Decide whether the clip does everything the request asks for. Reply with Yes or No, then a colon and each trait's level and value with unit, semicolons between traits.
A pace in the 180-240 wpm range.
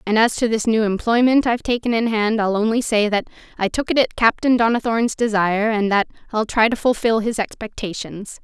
Yes: fast, 205 wpm